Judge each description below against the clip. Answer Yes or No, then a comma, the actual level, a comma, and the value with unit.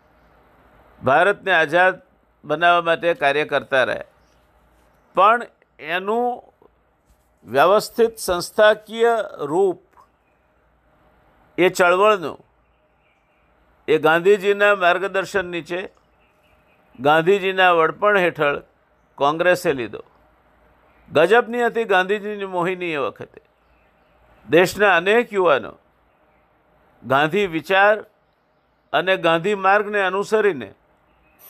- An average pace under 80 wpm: Yes, slow, 70 wpm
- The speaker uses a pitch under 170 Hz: No, high, 190 Hz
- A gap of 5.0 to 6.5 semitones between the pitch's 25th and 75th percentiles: No, average, 3.4 semitones